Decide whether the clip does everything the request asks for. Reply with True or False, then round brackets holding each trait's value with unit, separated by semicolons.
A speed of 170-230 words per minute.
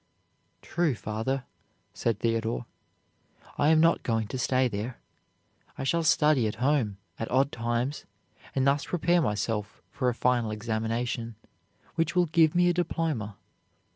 False (140 wpm)